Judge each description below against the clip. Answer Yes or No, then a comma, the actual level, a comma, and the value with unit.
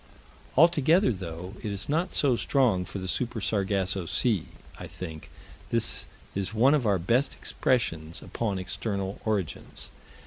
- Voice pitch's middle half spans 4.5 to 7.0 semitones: Yes, average, 5.2 semitones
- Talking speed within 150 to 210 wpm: No, average, 140 wpm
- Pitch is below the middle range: Yes, low, 100 Hz